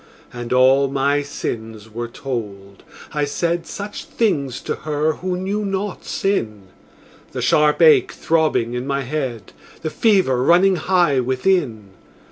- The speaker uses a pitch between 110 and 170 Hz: Yes, medium, 140 Hz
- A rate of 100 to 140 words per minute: Yes, slow, 135 wpm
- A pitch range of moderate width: No, wide, 6.2 semitones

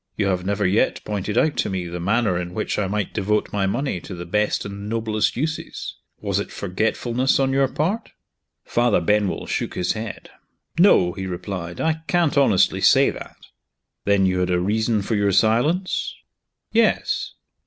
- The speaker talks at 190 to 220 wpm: No, average, 175 wpm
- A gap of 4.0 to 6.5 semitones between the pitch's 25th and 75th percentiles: Yes, average, 4.5 semitones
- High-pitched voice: No, low, 105 Hz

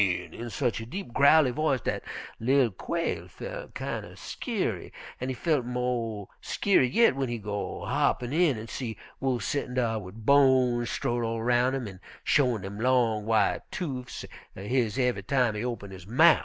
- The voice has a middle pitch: No, low, 125 Hz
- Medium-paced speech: Yes, average, 180 wpm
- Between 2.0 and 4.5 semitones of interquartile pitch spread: Yes, average, 3.4 semitones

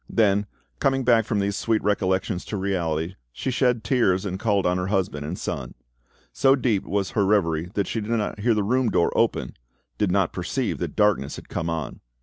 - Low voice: Yes, low, 100 Hz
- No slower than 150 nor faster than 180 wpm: No, average, 200 wpm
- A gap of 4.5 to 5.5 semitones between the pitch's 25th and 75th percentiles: No, average, 3.6 semitones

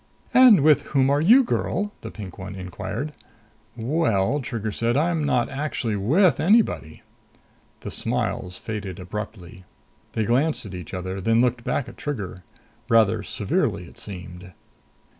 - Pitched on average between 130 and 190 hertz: No, low, 115 Hz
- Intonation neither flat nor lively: No, wide, 7.3 semitones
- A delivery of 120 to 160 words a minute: Yes, average, 140 wpm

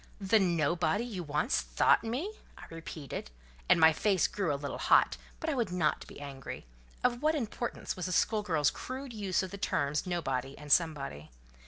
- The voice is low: No, medium, 180 Hz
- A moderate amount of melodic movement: No, wide, 6.9 semitones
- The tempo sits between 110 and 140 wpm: No, average, 185 wpm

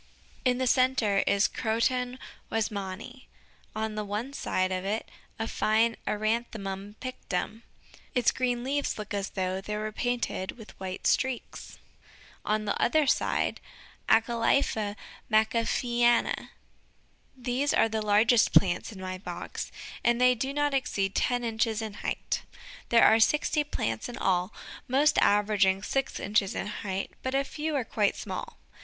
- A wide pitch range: No, average, 3.6 semitones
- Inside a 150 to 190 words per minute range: No, average, 140 wpm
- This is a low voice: No, high, 225 Hz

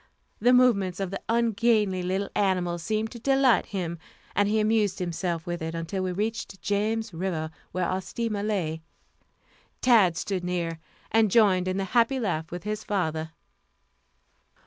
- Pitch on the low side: No, high, 195 Hz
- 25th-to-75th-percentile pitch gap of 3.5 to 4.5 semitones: Yes, average, 3.8 semitones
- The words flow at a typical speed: Yes, average, 155 wpm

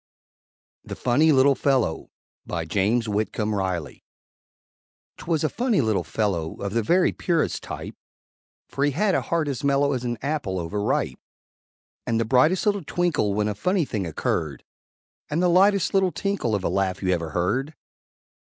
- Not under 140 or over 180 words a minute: Yes, average, 165 wpm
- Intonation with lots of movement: Yes, wide, 8.2 semitones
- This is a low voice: Yes, low, 125 Hz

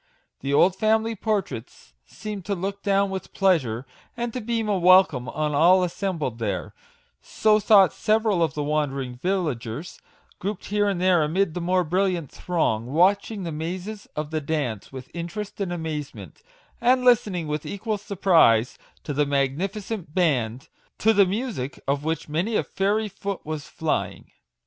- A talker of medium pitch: Yes, medium, 180 Hz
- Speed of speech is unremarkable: Yes, average, 165 wpm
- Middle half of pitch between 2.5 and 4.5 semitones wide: No, average, 5.2 semitones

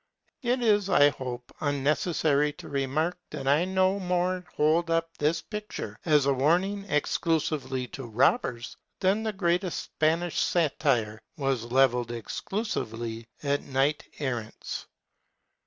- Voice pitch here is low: No, medium, 150 Hz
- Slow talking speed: Yes, slow, 125 wpm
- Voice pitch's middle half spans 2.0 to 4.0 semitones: No, average, 5.1 semitones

